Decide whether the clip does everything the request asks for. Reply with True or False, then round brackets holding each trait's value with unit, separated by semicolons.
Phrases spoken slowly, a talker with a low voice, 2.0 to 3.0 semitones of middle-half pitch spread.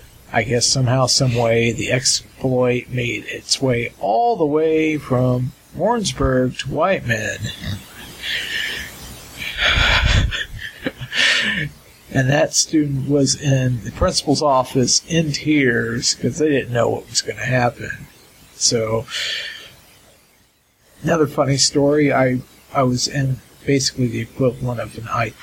True (120 wpm; 130 Hz; 2.7 semitones)